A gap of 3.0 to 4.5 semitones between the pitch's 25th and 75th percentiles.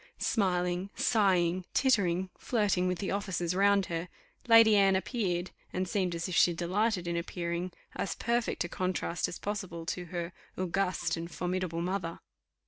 No: narrow, 2.4 semitones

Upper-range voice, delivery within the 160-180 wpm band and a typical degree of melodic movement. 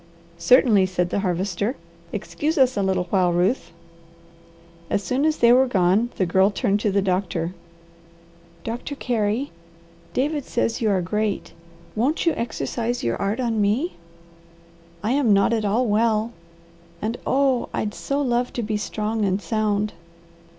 No: high, 215 Hz; average, 150 wpm; average, 3.8 semitones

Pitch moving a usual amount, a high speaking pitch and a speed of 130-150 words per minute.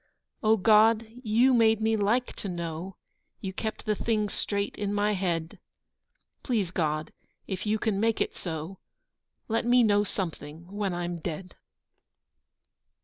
Yes: average, 3.9 semitones; high, 205 Hz; average, 145 wpm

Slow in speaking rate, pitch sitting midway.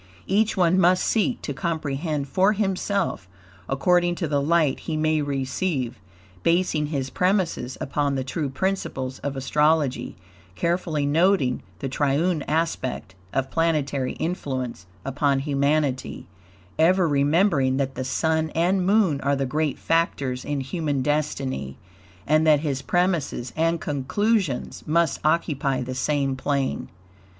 Yes: slow, 130 wpm; medium, 150 Hz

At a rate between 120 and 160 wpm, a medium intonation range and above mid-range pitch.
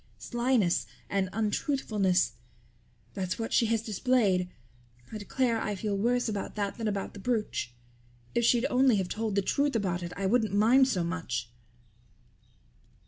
Yes: average, 150 wpm; average, 3.8 semitones; high, 210 Hz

